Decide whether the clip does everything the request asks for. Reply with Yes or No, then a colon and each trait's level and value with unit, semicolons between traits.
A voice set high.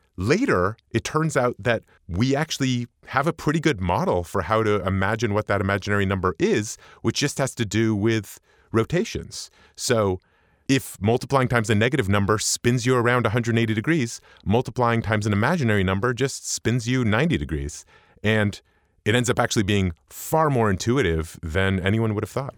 No: low, 115 Hz